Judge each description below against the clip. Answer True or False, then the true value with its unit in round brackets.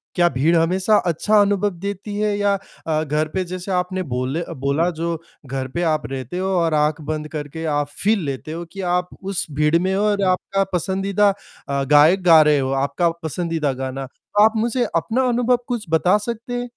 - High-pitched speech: False (170 Hz)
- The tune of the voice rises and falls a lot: False (4.7 semitones)